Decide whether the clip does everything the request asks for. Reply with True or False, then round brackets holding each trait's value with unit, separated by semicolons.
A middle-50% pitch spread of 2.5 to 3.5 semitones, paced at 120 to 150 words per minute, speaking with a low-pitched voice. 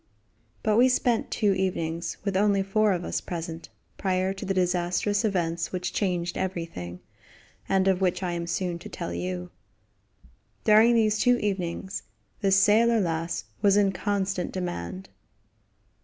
False (3.1 semitones; 145 wpm; 190 Hz)